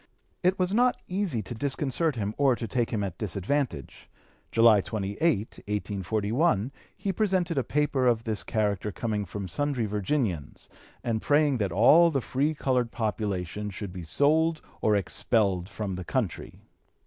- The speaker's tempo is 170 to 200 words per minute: No, average, 150 wpm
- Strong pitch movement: Yes, wide, 6.1 semitones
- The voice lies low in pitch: Yes, low, 115 Hz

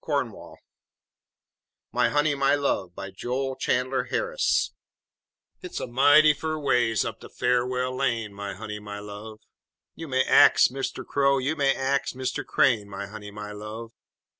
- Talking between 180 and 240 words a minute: No, average, 150 wpm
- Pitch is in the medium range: No, low, 125 Hz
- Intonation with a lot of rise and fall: No, average, 4.6 semitones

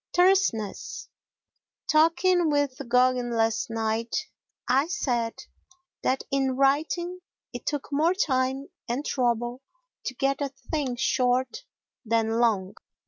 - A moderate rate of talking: No, slow, 110 wpm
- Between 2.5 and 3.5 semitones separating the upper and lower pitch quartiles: No, average, 4.0 semitones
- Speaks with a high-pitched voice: Yes, very high, 260 Hz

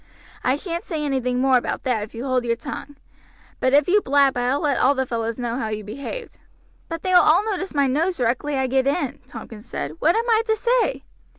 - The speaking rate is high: Yes, fast, 230 wpm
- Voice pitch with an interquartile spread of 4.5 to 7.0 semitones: Yes, average, 5.2 semitones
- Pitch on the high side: Yes, very high, 270 Hz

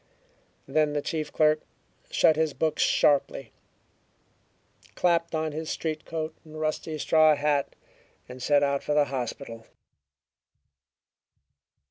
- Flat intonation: Yes, narrow, 1.8 semitones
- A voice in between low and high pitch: Yes, medium, 155 Hz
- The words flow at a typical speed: No, slow, 115 wpm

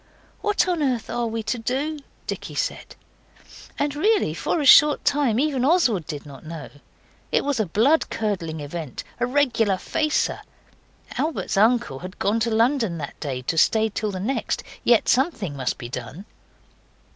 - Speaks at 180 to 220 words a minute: No, average, 165 wpm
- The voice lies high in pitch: Yes, high, 225 Hz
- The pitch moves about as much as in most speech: No, wide, 8.4 semitones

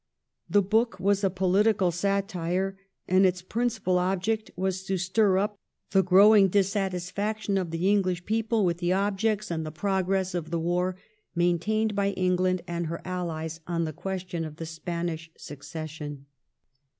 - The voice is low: No, medium, 185 Hz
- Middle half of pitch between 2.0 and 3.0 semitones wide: Yes, narrow, 2.5 semitones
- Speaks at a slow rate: No, average, 150 wpm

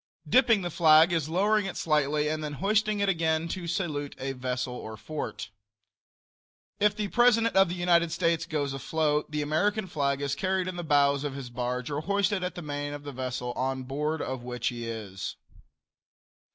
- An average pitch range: Yes, average, 5.0 semitones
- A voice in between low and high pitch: Yes, medium, 155 Hz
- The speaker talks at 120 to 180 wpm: No, average, 190 wpm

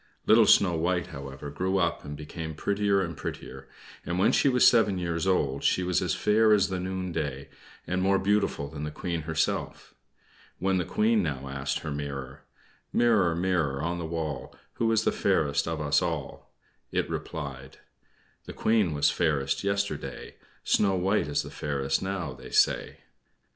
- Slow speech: No, average, 170 wpm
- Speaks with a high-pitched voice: No, very low, 85 Hz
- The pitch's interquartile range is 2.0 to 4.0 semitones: No, average, 4.8 semitones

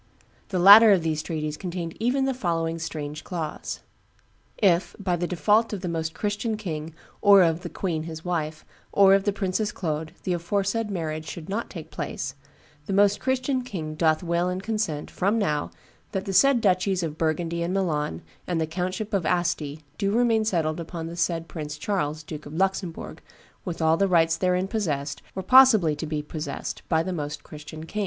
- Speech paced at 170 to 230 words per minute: Yes, average, 185 wpm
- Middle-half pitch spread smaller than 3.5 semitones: No, average, 3.9 semitones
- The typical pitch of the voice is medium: Yes, medium, 175 Hz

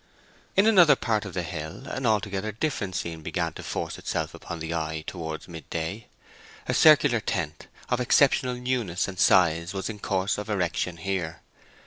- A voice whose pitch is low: Yes, very low, 95 Hz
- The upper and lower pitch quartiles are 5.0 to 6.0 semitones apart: Yes, wide, 5.6 semitones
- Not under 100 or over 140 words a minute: No, average, 165 wpm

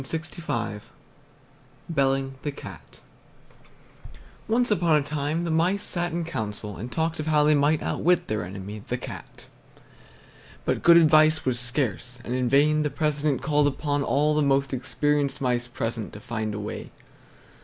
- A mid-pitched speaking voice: Yes, medium, 145 Hz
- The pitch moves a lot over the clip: No, average, 4.0 semitones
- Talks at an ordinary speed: Yes, average, 155 wpm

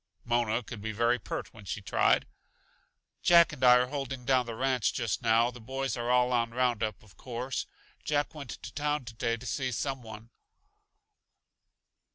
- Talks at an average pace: Yes, average, 175 wpm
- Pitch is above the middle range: No, low, 125 Hz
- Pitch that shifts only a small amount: Yes, narrow, 2.3 semitones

